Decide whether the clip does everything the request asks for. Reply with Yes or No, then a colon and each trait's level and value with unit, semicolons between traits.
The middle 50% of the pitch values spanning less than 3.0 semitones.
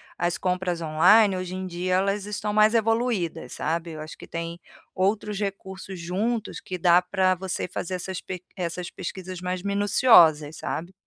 Yes: narrow, 2.5 semitones